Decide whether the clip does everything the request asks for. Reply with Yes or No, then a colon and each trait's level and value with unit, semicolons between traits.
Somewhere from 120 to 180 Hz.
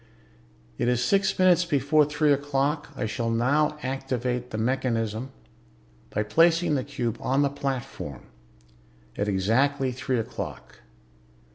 Yes: low, 135 Hz